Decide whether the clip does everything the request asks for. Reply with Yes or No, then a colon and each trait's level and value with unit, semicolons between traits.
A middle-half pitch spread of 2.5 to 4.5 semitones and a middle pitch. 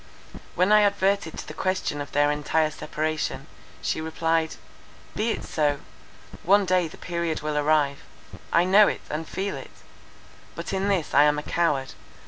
Yes: average, 4.1 semitones; medium, 160 Hz